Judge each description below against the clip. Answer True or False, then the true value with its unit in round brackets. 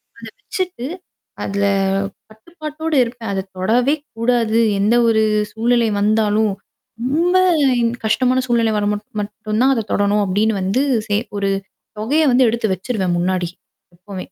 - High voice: True (220 Hz)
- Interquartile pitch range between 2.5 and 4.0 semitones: True (3.4 semitones)